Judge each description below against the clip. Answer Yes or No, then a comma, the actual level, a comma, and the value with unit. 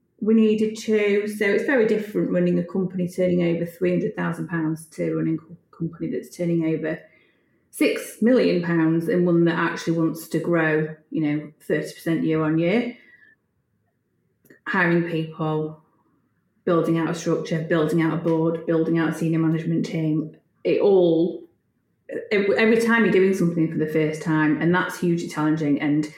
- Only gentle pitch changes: Yes, narrow, 2.0 semitones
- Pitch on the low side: No, medium, 165 Hz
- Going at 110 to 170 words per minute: Yes, average, 160 wpm